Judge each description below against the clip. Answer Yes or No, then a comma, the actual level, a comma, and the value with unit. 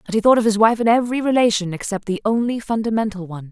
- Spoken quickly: Yes, fast, 240 wpm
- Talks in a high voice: Yes, high, 215 Hz